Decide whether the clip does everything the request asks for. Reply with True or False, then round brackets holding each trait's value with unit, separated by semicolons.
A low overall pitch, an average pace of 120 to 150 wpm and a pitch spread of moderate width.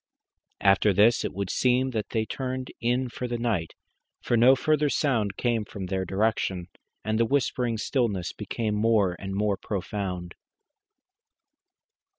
True (110 Hz; 145 wpm; 3.9 semitones)